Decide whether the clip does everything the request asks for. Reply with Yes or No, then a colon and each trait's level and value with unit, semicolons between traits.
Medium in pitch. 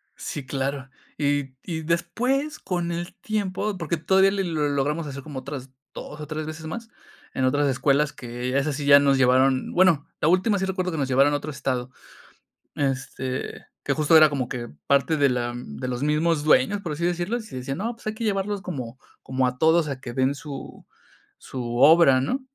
Yes: medium, 145 Hz